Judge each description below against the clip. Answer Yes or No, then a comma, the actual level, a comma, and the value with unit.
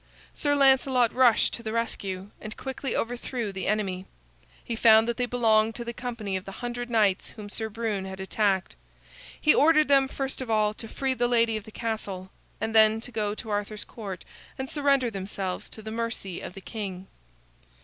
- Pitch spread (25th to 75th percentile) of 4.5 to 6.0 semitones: No, average, 3.0 semitones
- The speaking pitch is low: No, high, 225 Hz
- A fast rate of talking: No, average, 190 wpm